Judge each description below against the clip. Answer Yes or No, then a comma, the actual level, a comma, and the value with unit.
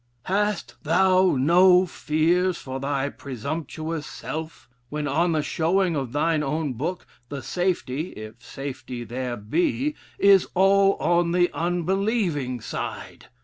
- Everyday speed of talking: No, slow, 125 wpm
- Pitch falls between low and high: Yes, medium, 160 Hz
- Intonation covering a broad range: No, average, 4.7 semitones